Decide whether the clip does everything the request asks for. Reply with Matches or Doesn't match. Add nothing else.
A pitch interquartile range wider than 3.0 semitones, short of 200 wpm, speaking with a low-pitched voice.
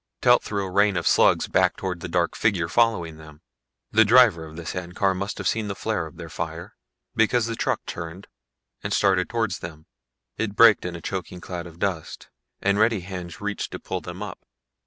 Doesn't match